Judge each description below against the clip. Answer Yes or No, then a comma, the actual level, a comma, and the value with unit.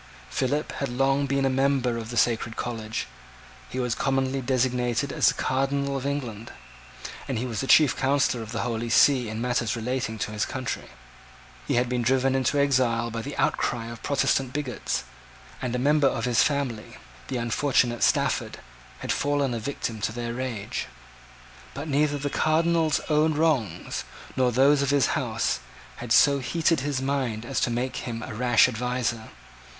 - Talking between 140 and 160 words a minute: No, average, 175 wpm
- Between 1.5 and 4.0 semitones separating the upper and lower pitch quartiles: Yes, average, 2.9 semitones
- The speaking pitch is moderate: No, low, 130 Hz